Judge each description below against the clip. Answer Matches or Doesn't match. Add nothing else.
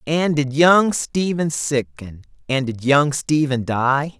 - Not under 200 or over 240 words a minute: Doesn't match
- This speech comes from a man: Matches